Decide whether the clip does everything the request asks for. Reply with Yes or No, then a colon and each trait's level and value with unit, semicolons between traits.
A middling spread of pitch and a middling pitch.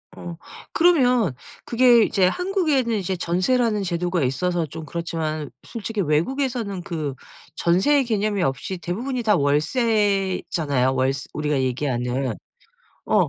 No: wide, 7.4 semitones; medium, 180 Hz